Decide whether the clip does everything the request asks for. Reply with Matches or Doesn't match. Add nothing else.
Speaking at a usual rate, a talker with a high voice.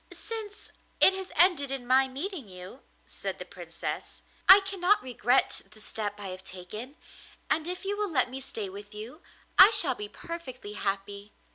Matches